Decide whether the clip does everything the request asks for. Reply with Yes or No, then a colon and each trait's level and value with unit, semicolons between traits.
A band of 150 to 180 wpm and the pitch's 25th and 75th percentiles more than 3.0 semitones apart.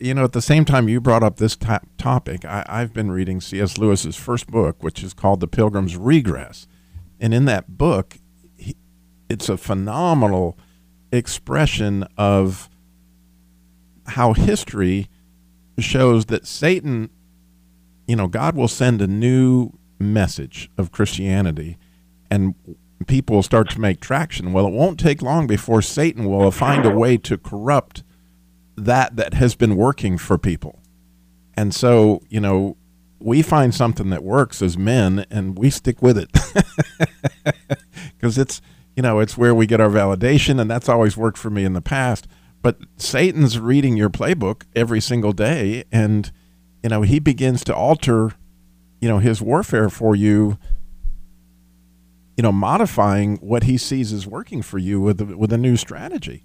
Yes: average, 155 wpm; wide, 5.4 semitones